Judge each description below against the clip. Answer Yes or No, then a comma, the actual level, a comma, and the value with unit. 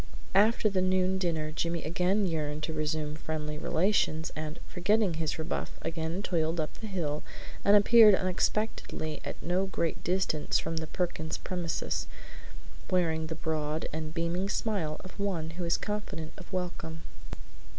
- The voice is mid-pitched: Yes, medium, 170 Hz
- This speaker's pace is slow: No, average, 150 wpm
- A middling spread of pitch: Yes, average, 3.1 semitones